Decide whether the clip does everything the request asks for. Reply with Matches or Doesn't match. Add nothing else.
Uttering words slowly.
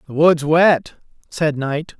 Doesn't match